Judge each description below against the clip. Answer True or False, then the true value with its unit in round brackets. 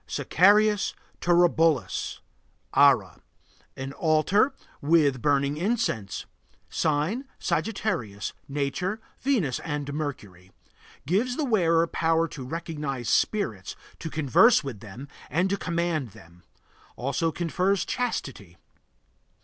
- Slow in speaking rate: True (100 wpm)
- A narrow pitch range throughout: False (5.4 semitones)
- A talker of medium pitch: True (160 Hz)